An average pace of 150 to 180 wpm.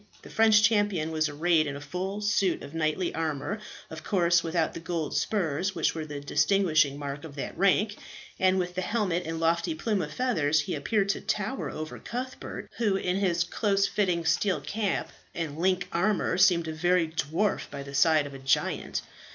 No: average, 190 wpm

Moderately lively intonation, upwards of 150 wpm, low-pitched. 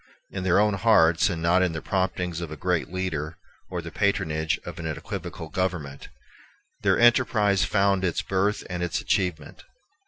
Yes: average, 3.1 semitones; average, 165 wpm; very low, 90 Hz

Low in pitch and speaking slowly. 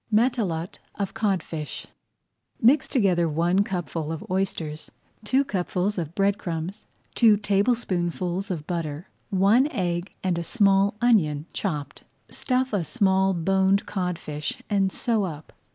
No: high, 190 Hz; slow, 125 wpm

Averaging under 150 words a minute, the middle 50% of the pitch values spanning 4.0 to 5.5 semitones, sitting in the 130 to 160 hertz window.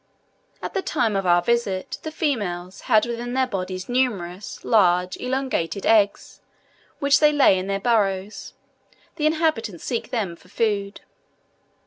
No: average, 140 wpm; average, 5.1 semitones; high, 215 Hz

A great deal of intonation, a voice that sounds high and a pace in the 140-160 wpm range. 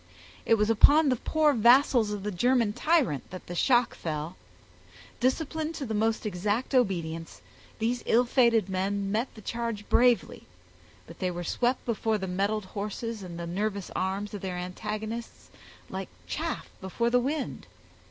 No: average, 4.2 semitones; high, 215 Hz; average, 155 wpm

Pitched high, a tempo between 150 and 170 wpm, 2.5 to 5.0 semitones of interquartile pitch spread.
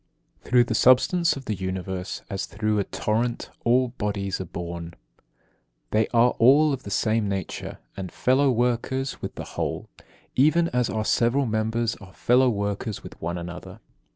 No: low, 110 Hz; average, 165 wpm; average, 4.2 semitones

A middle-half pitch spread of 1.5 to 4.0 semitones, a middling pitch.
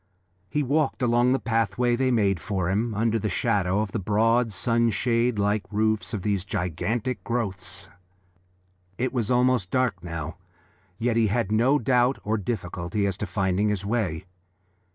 No: average, 3.6 semitones; low, 110 Hz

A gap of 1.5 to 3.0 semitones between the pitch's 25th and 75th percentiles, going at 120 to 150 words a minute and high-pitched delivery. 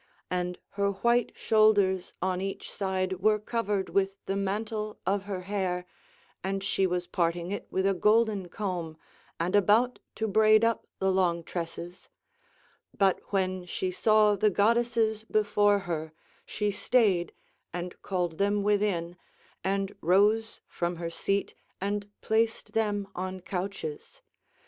Yes: narrow, 2.6 semitones; slow, 135 wpm; high, 195 Hz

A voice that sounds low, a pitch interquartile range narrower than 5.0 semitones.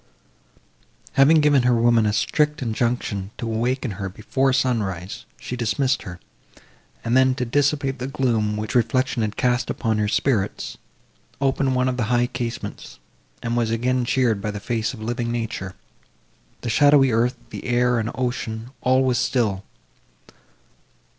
Yes: low, 120 Hz; average, 2.7 semitones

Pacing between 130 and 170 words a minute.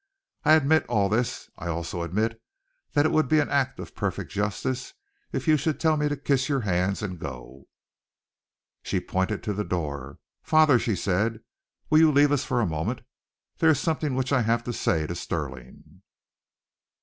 No: average, 185 wpm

